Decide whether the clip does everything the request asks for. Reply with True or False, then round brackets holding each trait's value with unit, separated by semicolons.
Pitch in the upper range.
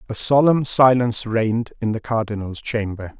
False (115 Hz)